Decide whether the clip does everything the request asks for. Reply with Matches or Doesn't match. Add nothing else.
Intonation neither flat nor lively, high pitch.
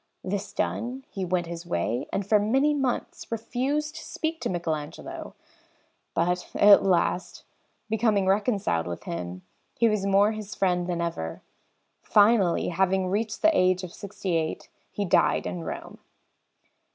Matches